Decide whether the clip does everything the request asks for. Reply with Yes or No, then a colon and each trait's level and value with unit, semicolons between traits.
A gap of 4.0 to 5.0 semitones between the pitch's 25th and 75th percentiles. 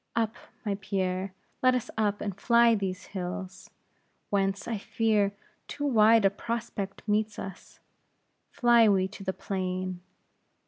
No: average, 2.9 semitones